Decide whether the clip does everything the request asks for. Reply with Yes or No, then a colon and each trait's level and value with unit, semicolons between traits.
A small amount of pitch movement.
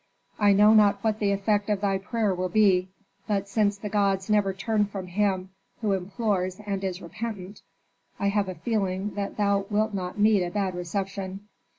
Yes: narrow, 1.6 semitones